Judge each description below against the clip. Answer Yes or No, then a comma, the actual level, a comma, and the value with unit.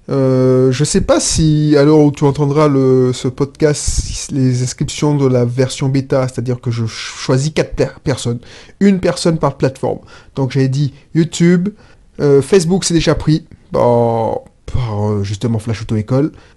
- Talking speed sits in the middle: Yes, average, 155 wpm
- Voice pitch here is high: No, low, 135 Hz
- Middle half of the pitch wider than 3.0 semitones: Yes, average, 3.6 semitones